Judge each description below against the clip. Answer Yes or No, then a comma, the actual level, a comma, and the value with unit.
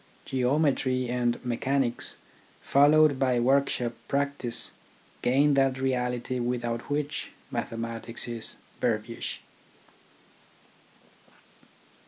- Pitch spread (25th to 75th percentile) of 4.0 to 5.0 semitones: No, narrow, 2.6 semitones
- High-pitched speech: No, low, 130 Hz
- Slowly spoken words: Yes, slow, 80 wpm